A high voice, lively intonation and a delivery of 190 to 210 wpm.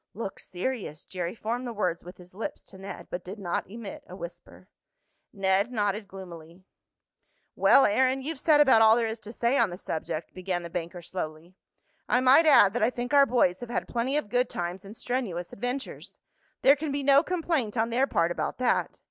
Yes: high, 220 Hz; wide, 5.9 semitones; average, 200 wpm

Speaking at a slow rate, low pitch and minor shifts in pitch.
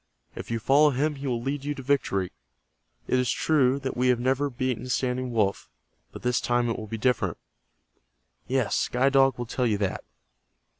No: average, 190 wpm; low, 125 Hz; narrow, 2.2 semitones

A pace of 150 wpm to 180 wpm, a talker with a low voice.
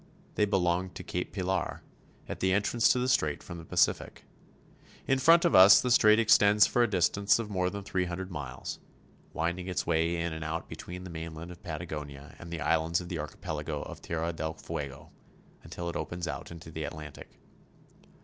No: average, 190 wpm; very low, 85 Hz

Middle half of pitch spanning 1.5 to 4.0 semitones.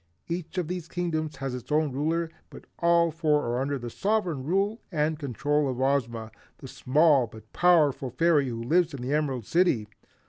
No: average, 4.5 semitones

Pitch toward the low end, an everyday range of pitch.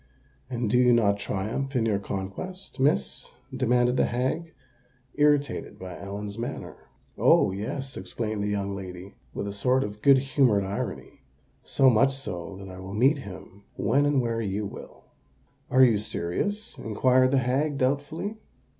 Yes: low, 120 Hz; average, 5.0 semitones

